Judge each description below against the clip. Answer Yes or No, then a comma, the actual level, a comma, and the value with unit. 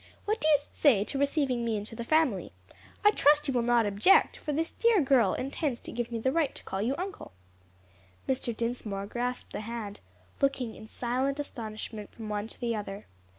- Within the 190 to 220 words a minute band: Yes, average, 195 wpm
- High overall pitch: Yes, high, 240 Hz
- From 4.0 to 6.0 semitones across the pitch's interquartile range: Yes, average, 4.5 semitones